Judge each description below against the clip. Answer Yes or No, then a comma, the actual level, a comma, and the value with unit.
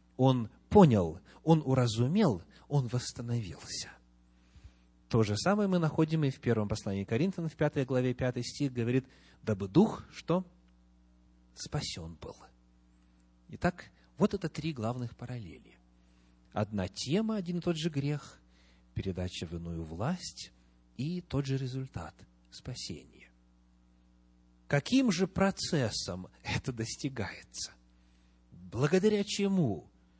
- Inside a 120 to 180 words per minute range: No, slow, 110 wpm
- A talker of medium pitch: No, low, 110 Hz